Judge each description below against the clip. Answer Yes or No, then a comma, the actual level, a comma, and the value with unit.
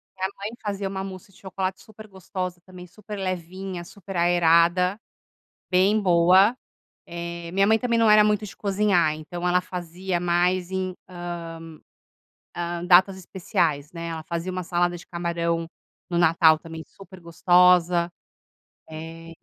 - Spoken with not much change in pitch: Yes, narrow, 2.0 semitones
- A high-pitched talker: No, medium, 180 Hz